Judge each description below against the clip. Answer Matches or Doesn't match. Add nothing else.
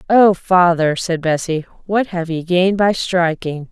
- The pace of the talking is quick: Doesn't match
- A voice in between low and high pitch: Matches